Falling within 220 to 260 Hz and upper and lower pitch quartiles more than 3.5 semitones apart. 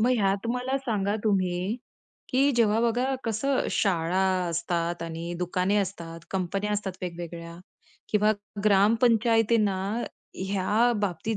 No: high, 200 Hz; average, 4.2 semitones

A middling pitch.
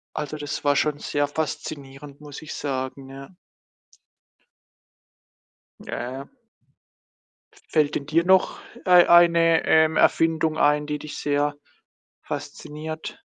Yes: medium, 150 Hz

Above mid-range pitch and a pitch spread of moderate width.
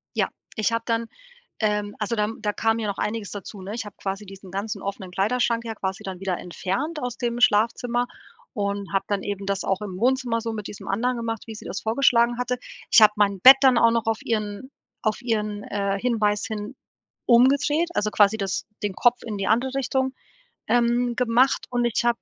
Yes: high, 220 Hz; average, 3.0 semitones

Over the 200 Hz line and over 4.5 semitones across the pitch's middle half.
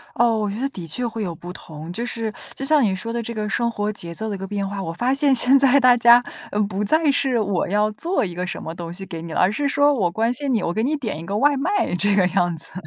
Yes: high, 215 Hz; average, 5.1 semitones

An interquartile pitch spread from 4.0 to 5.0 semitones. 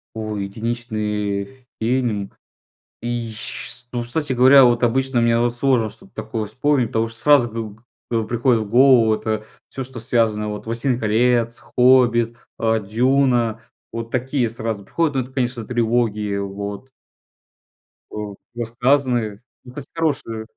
No: narrow, 2.5 semitones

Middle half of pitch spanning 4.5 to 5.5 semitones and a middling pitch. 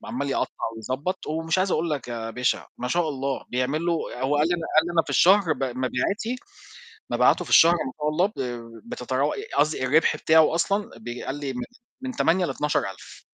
Yes: average, 5.0 semitones; medium, 150 Hz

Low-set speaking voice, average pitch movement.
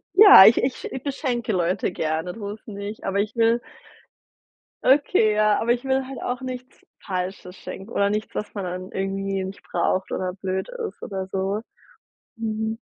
No: high, 210 Hz; average, 3.8 semitones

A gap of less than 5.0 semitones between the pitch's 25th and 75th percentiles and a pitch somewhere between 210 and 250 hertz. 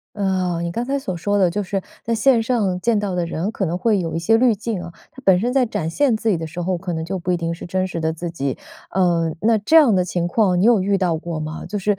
No: average, 4.1 semitones; medium, 185 Hz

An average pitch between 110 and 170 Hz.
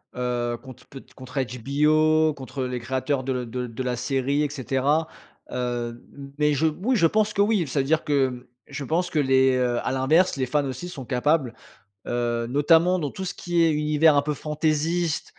Yes: medium, 140 Hz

